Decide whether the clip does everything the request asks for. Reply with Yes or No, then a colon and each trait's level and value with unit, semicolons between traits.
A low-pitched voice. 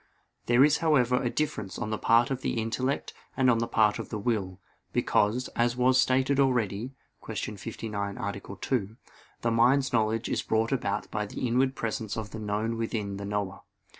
Yes: low, 115 Hz